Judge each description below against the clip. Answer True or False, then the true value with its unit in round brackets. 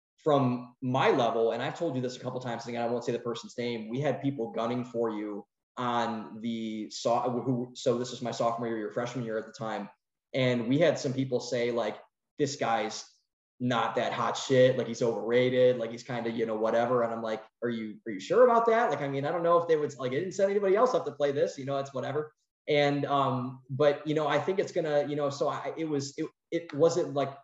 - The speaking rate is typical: False (250 wpm)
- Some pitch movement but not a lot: True (3.5 semitones)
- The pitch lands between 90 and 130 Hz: True (125 Hz)